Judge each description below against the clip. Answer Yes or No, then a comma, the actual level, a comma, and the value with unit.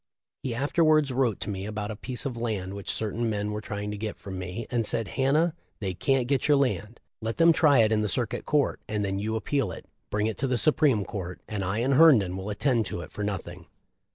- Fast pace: Yes, fast, 240 wpm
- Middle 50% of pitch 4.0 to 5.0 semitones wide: Yes, average, 4.6 semitones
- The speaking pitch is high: No, low, 110 Hz